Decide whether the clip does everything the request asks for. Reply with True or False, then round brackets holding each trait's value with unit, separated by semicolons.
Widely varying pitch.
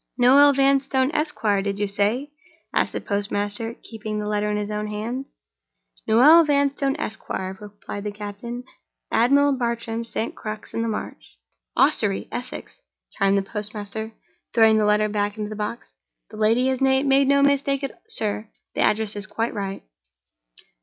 False (4.2 semitones)